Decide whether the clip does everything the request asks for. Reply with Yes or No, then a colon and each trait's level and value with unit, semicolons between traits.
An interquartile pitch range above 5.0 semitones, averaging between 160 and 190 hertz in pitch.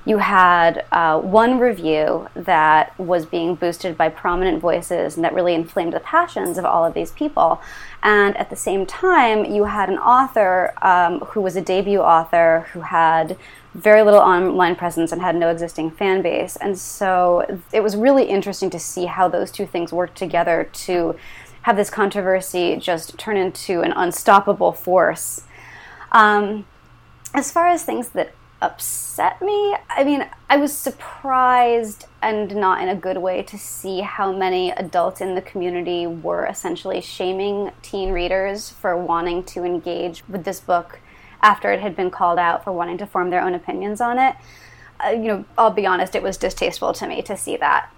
No: average, 3.0 semitones; medium, 185 Hz